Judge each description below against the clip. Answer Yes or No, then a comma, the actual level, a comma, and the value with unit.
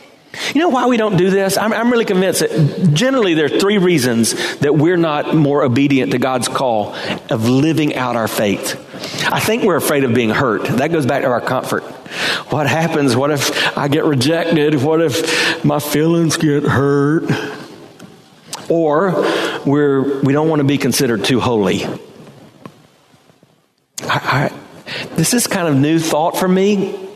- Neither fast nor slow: Yes, average, 170 wpm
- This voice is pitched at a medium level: Yes, medium, 155 Hz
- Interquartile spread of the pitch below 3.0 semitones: No, average, 3.8 semitones